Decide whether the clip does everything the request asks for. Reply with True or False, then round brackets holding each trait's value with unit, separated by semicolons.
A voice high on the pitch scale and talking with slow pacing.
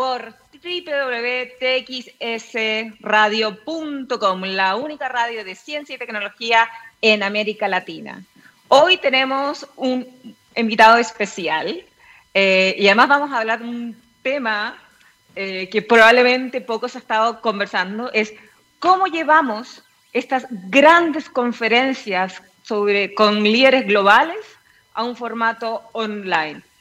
True (235 Hz; 105 wpm)